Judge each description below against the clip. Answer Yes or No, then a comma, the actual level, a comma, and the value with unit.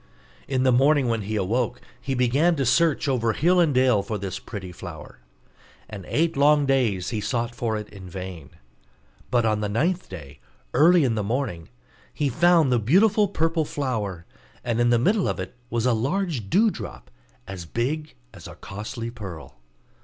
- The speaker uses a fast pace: No, average, 175 wpm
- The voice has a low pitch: Yes, low, 120 Hz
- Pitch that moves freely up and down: Yes, wide, 6.1 semitones